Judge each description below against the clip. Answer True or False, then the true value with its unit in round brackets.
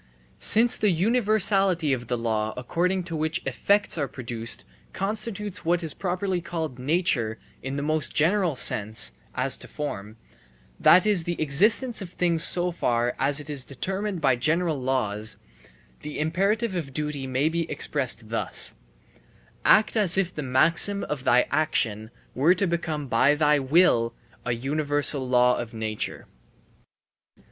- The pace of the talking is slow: False (150 wpm)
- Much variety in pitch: True (6.0 semitones)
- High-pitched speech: False (155 Hz)